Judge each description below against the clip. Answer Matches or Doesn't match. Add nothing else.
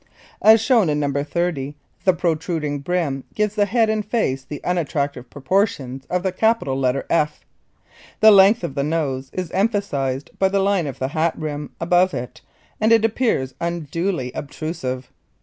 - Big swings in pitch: Matches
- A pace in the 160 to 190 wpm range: Matches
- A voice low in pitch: Doesn't match